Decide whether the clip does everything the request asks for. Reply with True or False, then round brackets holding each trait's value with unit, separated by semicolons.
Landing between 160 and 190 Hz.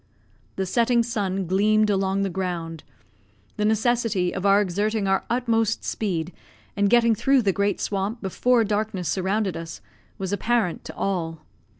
False (200 Hz)